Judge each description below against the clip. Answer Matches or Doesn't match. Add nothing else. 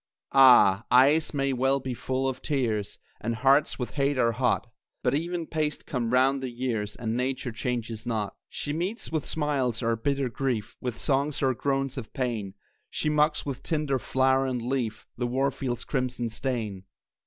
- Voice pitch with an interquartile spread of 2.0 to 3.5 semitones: Matches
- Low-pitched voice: Matches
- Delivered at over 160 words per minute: Matches